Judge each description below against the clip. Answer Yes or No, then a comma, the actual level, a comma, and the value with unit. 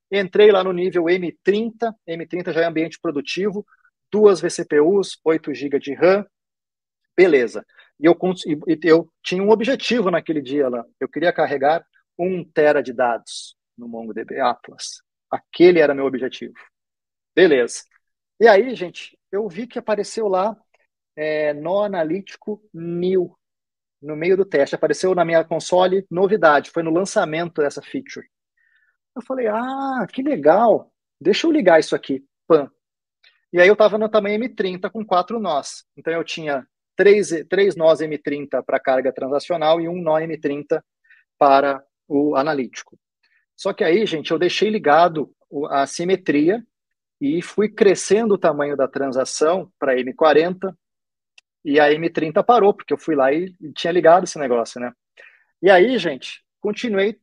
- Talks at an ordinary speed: Yes, average, 145 wpm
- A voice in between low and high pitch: Yes, medium, 170 Hz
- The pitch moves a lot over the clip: Yes, wide, 5.7 semitones